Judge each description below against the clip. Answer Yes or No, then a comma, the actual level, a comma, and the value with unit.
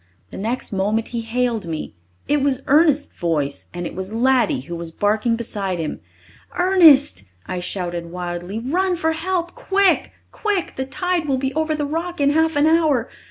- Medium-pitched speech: No, very high, 260 Hz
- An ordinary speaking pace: Yes, average, 175 wpm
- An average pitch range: No, wide, 8.9 semitones